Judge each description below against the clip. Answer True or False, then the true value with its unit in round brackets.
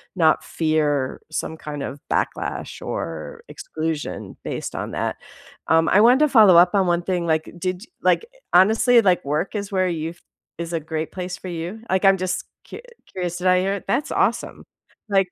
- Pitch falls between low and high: True (180 Hz)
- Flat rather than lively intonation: False (3.2 semitones)